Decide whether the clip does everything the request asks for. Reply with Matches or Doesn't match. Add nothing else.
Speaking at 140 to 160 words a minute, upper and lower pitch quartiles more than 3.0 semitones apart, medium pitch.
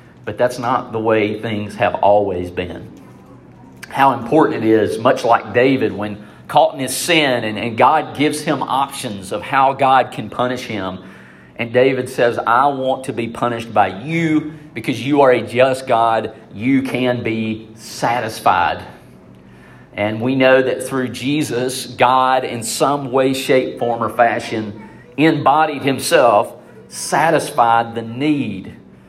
Doesn't match